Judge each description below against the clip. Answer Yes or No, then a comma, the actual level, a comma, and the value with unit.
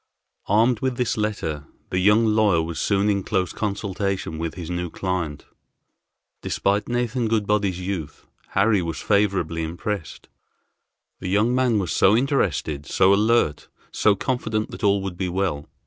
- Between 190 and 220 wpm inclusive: No, average, 145 wpm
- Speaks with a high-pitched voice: No, low, 100 Hz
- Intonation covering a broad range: No, average, 3.6 semitones